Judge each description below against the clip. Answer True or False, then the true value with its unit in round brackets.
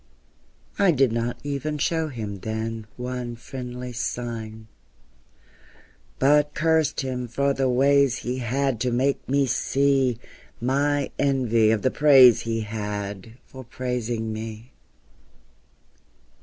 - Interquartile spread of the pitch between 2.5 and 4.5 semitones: True (3.5 semitones)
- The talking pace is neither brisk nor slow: False (115 wpm)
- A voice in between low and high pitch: False (125 Hz)